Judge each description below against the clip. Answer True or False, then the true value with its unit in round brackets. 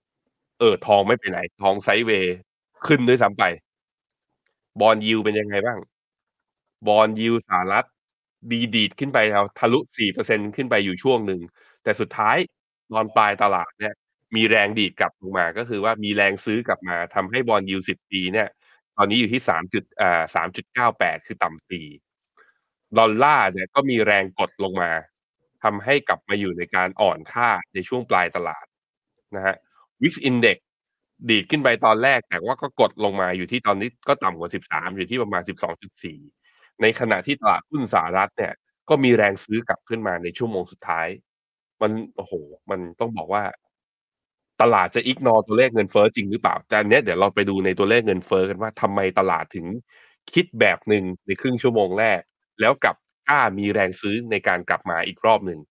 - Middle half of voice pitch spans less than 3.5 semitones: True (2.9 semitones)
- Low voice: True (105 Hz)